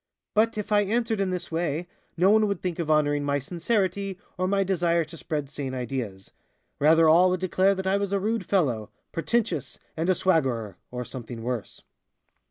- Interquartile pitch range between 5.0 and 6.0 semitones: Yes, wide, 5.5 semitones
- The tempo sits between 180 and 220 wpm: Yes, average, 185 wpm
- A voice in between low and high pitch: Yes, medium, 170 Hz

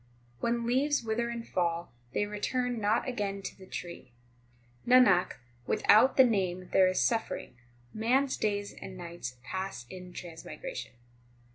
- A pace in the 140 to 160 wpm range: Yes, average, 145 wpm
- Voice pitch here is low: No, high, 205 Hz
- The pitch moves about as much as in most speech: Yes, average, 4.6 semitones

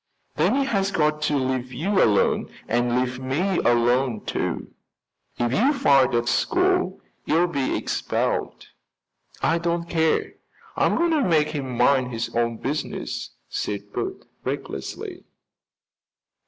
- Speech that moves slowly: Yes, slow, 130 wpm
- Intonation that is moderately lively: No, wide, 6.1 semitones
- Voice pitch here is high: No, medium, 140 Hz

